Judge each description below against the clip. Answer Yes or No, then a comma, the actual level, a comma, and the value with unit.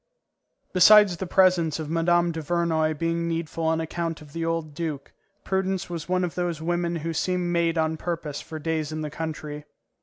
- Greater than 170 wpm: Yes, average, 180 wpm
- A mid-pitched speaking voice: Yes, medium, 165 Hz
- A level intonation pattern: Yes, narrow, 1.7 semitones